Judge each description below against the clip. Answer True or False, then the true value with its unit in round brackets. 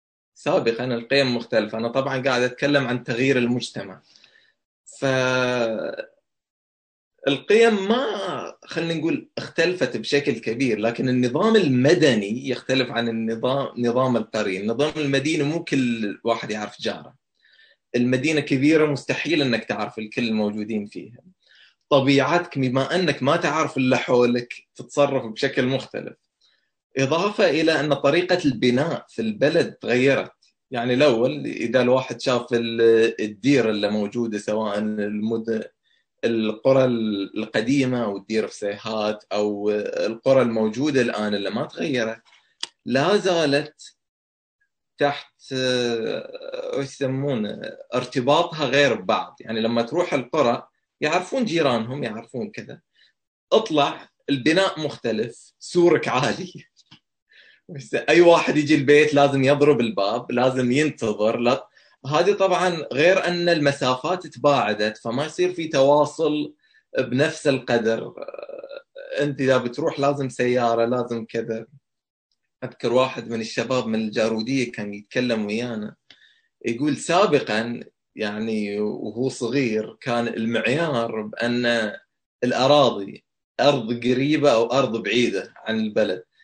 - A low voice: True (125 Hz)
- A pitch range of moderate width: True (4.1 semitones)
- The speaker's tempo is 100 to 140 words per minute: True (110 wpm)